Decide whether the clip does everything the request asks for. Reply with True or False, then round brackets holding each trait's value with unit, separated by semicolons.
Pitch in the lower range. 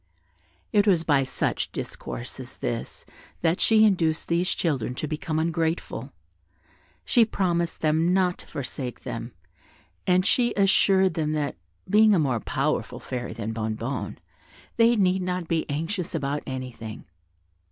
False (165 Hz)